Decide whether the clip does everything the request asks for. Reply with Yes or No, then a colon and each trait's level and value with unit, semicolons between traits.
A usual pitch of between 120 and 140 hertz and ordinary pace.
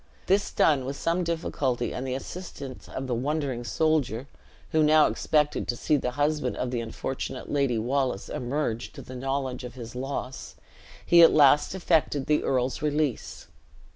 Yes: low, 135 Hz; average, 165 wpm